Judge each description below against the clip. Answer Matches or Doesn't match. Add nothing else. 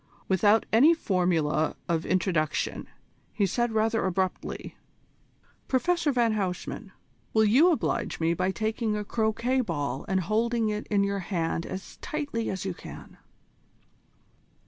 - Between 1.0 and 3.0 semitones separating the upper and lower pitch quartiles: Doesn't match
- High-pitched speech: Matches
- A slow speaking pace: Matches